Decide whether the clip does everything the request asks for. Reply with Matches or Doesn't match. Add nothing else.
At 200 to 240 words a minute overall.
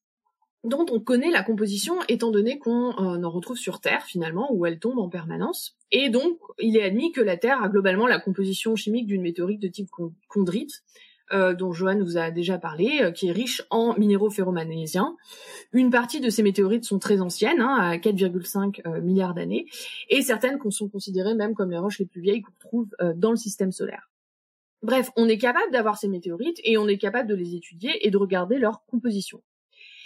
Matches